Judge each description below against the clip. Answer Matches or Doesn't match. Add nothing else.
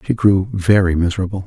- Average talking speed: Matches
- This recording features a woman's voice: Doesn't match